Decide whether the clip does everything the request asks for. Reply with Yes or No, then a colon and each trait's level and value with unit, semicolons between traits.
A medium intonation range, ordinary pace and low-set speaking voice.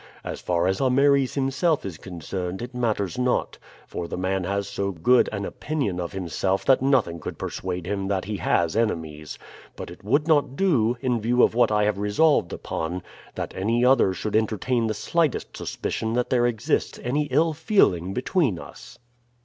No: wide, 5.7 semitones; average, 180 wpm; low, 110 Hz